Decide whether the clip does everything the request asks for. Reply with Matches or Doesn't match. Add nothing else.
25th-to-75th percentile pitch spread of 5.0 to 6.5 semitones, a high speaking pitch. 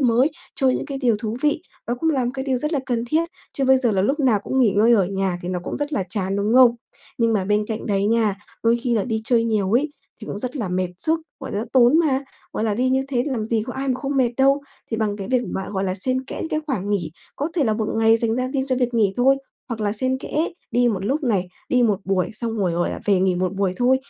Doesn't match